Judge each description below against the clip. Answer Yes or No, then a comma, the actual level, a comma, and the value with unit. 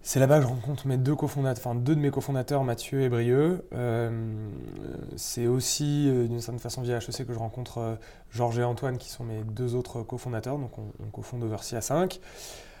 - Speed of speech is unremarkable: Yes, average, 200 wpm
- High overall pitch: No, low, 125 Hz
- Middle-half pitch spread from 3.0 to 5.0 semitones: No, narrow, 2.6 semitones